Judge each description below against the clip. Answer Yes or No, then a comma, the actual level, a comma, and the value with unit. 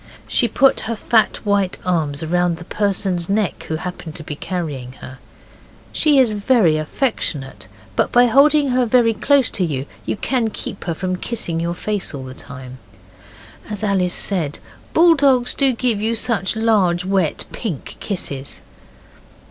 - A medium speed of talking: Yes, average, 155 wpm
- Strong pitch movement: Yes, wide, 6.0 semitones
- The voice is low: No, high, 195 Hz